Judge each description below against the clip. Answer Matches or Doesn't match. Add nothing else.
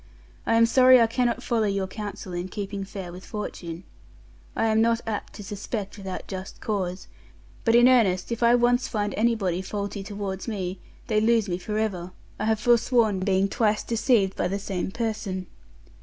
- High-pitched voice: Matches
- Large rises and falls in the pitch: Doesn't match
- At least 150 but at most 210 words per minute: Matches